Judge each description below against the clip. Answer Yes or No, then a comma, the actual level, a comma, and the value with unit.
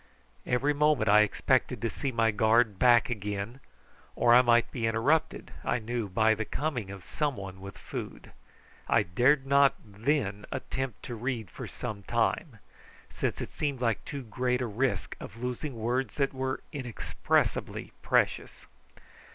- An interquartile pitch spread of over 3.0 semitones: Yes, average, 3.5 semitones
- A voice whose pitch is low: Yes, low, 120 Hz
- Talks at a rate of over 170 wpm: No, average, 155 wpm